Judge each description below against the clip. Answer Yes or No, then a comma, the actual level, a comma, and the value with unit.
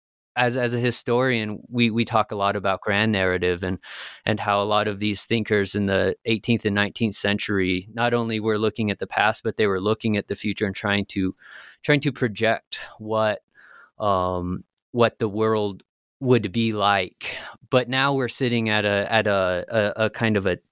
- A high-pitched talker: No, low, 110 Hz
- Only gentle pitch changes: Yes, narrow, 2.3 semitones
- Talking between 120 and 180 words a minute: No, average, 195 wpm